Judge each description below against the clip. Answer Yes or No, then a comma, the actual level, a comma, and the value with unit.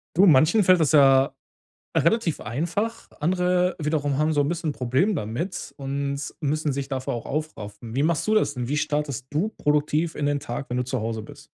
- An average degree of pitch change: Yes, average, 3.7 semitones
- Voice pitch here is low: No, medium, 145 Hz